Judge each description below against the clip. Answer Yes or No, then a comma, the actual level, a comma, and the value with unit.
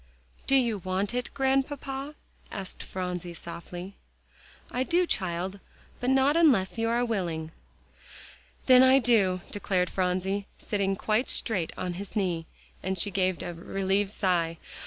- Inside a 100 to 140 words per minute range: Yes, slow, 135 wpm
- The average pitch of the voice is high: Yes, high, 195 Hz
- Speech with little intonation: No, average, 5.2 semitones